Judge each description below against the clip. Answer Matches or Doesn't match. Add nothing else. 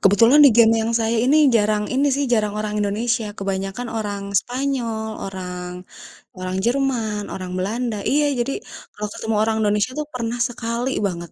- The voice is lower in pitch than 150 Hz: Doesn't match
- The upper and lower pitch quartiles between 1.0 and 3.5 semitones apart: Matches